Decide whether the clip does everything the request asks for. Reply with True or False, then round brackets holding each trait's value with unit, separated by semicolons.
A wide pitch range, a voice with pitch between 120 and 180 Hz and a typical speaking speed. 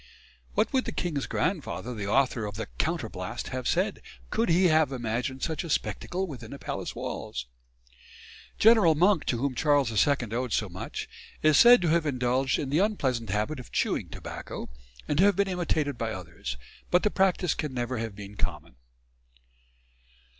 True (7.0 semitones; 140 Hz; 175 wpm)